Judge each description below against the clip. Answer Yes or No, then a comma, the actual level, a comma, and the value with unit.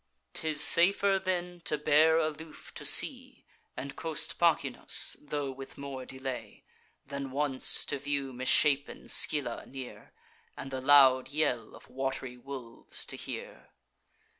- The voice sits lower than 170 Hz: Yes, medium, 140 Hz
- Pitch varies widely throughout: No, average, 2.8 semitones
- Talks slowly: Yes, slow, 130 wpm